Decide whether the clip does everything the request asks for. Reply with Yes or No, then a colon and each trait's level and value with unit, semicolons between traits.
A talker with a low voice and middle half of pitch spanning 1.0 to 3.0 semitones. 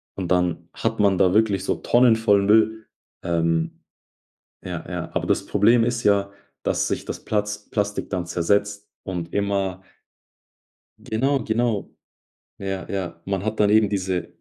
Yes: low, 100 Hz; average, 2.7 semitones